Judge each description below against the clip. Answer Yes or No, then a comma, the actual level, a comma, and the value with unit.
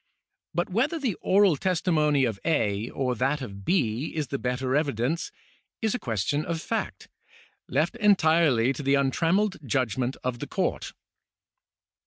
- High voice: No, medium, 145 Hz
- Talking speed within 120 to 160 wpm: Yes, average, 145 wpm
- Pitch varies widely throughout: Yes, wide, 5.7 semitones